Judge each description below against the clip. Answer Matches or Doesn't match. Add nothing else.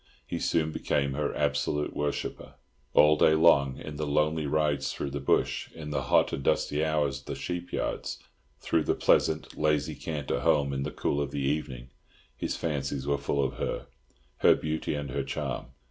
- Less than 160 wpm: Doesn't match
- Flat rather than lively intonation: Matches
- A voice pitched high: Doesn't match